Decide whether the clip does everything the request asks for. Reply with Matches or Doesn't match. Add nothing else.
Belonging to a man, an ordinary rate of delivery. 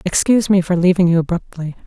Doesn't match